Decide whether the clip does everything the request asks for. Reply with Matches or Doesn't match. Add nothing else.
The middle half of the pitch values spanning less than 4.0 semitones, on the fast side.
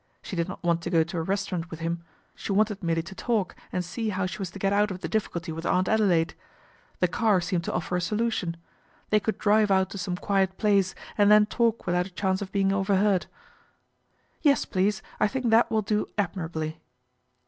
Matches